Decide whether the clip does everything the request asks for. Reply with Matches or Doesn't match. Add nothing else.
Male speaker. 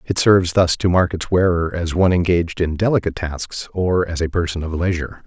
Matches